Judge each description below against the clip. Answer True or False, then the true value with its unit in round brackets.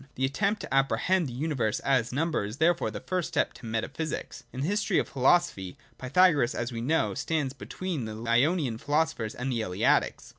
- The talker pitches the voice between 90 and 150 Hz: True (135 Hz)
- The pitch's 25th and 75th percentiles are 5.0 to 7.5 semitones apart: True (5.6 semitones)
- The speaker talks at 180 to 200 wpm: True (185 wpm)